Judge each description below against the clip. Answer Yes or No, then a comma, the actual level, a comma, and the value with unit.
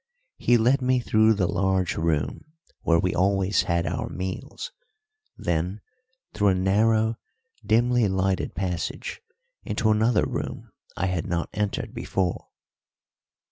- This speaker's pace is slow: Yes, slow, 125 wpm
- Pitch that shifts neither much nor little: Yes, average, 3.4 semitones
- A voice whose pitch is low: Yes, very low, 95 Hz